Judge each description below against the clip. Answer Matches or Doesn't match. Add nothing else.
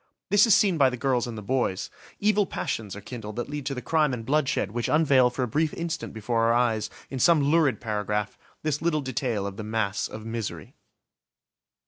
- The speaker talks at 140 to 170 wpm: Doesn't match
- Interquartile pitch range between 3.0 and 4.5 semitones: Doesn't match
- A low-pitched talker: Matches